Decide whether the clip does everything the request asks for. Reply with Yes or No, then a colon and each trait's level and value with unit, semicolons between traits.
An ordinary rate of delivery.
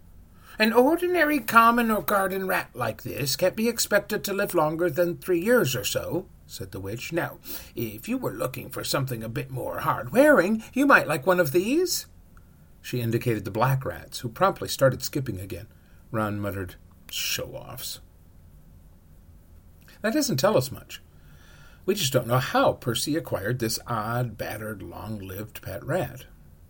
Yes: average, 165 wpm